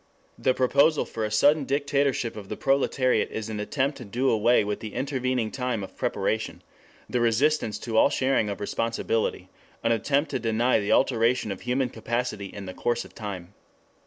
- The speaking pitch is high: No, low, 120 Hz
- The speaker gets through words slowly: No, average, 180 wpm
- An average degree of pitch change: Yes, average, 3.6 semitones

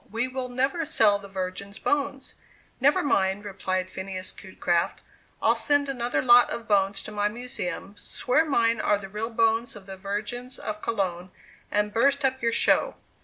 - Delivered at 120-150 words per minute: No, average, 170 wpm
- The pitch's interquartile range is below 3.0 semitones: No, average, 4.3 semitones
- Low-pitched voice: No, high, 220 Hz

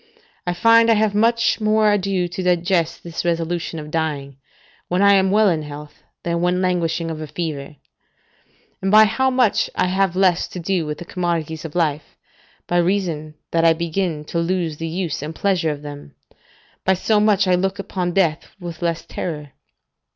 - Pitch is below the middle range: No, medium, 175 Hz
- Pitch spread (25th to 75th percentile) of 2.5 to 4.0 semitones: Yes, average, 3.2 semitones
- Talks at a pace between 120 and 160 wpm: No, average, 185 wpm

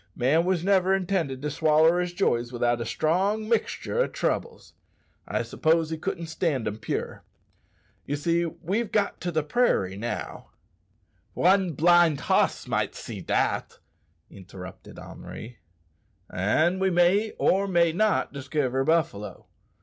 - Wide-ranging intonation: Yes, wide, 5.9 semitones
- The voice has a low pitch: No, medium, 165 Hz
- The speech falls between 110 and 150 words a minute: Yes, average, 140 wpm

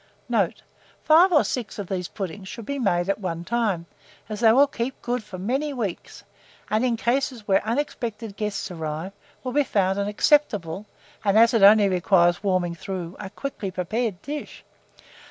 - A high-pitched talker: Yes, high, 210 Hz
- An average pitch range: Yes, average, 4.3 semitones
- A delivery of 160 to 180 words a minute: Yes, average, 170 wpm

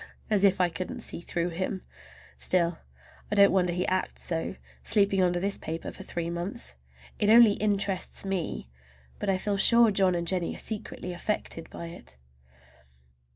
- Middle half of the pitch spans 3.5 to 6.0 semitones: No, narrow, 2.5 semitones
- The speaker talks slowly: No, average, 165 wpm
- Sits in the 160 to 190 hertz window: Yes, medium, 185 Hz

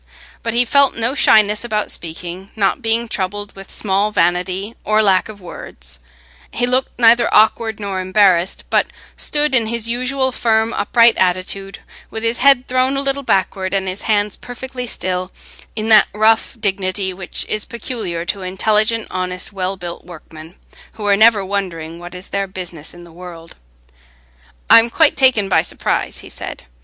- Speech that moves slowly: No, average, 165 wpm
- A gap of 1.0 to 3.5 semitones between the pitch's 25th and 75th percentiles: No, average, 3.9 semitones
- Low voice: No, high, 205 Hz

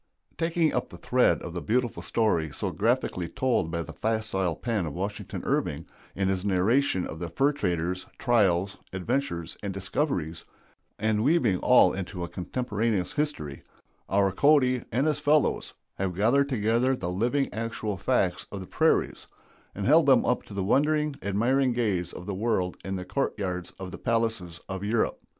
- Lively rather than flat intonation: Yes, wide, 5.7 semitones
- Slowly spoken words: No, average, 170 wpm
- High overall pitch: No, low, 105 Hz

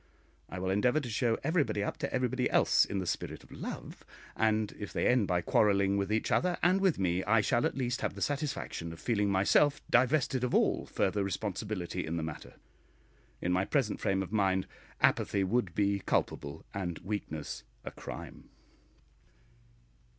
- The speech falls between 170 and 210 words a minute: Yes, average, 175 wpm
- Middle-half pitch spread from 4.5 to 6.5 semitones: Yes, average, 4.8 semitones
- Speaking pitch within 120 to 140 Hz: No, low, 105 Hz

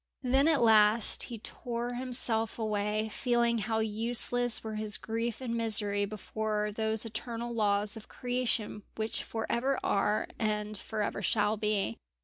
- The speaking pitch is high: Yes, high, 220 Hz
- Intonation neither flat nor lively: No, narrow, 2.1 semitones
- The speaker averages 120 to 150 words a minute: Yes, average, 145 wpm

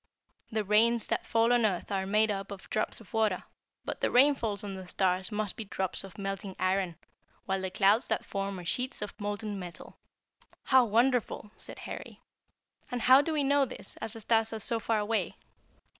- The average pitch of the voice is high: Yes, high, 210 Hz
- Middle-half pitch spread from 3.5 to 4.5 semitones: No, average, 2.9 semitones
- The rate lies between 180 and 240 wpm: Yes, average, 195 wpm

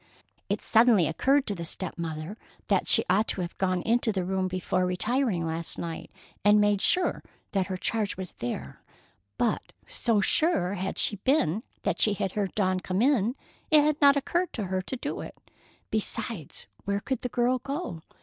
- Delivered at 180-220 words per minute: Yes, average, 185 wpm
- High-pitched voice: Yes, high, 200 Hz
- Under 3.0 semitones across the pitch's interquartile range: No, average, 5.0 semitones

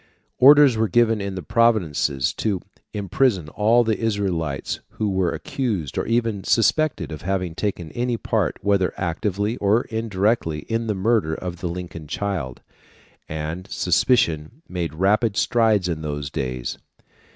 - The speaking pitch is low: Yes, low, 100 Hz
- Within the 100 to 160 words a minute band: Yes, average, 140 wpm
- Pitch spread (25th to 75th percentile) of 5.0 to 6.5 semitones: Yes, average, 5.3 semitones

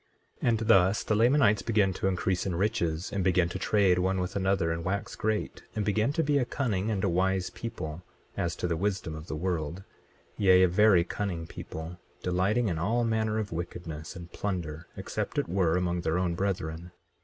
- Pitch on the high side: No, very low, 95 Hz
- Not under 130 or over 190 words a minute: No, average, 200 wpm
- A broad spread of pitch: No, average, 3.3 semitones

